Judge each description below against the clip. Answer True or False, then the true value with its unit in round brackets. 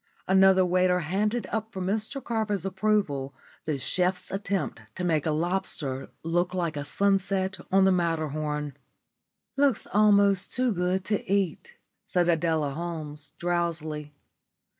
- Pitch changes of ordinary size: True (3.9 semitones)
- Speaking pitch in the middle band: True (180 Hz)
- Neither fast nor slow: False (130 wpm)